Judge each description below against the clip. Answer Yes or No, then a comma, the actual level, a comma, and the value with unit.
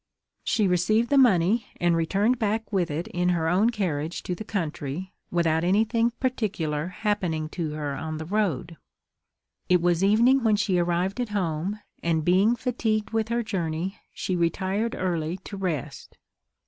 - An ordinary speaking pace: Yes, average, 160 wpm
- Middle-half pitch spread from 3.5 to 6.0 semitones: Yes, average, 4.5 semitones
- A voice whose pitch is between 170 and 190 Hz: Yes, medium, 185 Hz